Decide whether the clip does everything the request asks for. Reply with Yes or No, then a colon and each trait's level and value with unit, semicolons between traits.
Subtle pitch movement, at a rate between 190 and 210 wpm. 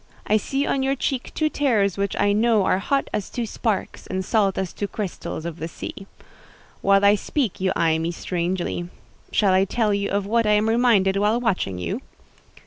No: average, 3.4 semitones; average, 200 wpm